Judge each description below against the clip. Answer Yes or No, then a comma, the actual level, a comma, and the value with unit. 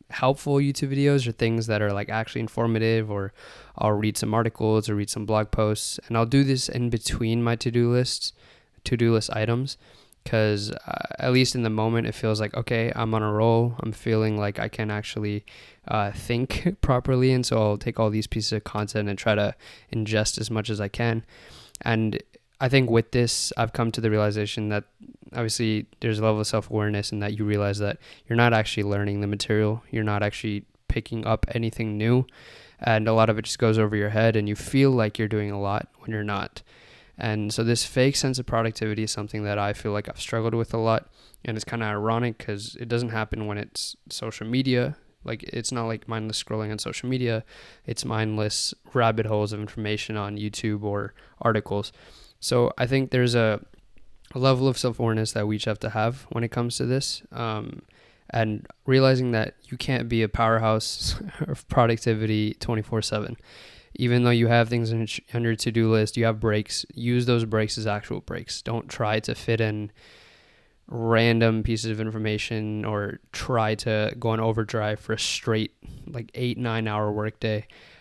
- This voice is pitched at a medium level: No, low, 110 Hz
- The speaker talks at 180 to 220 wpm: Yes, average, 200 wpm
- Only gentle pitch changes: Yes, narrow, 1.8 semitones